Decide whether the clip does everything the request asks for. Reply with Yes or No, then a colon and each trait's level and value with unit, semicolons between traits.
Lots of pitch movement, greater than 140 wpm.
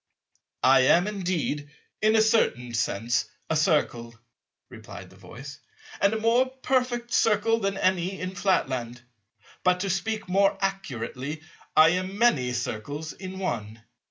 No: wide, 7.8 semitones; slow, 135 wpm